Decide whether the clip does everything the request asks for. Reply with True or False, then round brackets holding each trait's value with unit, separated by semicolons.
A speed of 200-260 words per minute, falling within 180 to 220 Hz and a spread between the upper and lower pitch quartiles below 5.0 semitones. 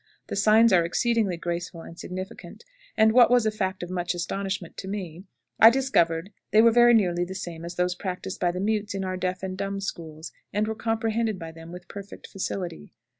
True (205 wpm; 190 Hz; 3.6 semitones)